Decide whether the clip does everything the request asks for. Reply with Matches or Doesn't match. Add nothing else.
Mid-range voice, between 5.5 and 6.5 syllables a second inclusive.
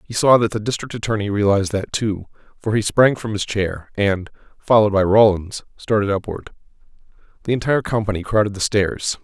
Doesn't match